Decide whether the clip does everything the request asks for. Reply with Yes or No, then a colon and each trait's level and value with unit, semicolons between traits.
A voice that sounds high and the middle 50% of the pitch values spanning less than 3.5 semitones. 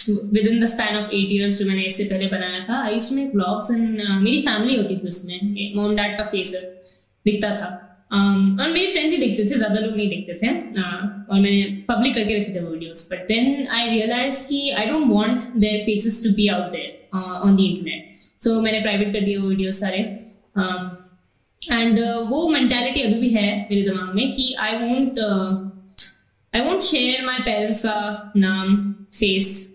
Yes: high, 210 Hz; average, 3.0 semitones